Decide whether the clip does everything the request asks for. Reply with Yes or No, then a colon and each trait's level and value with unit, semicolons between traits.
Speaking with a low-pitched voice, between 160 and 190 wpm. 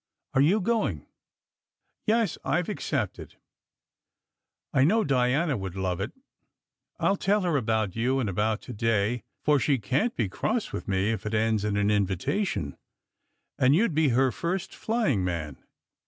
Yes: low, 125 Hz; average, 175 wpm